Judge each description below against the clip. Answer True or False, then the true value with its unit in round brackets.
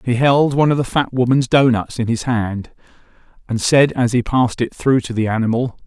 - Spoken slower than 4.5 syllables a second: False (5.4 syllables/s)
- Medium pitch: False (125 Hz)